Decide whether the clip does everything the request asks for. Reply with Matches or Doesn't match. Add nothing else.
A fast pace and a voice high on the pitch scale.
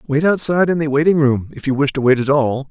Doesn't match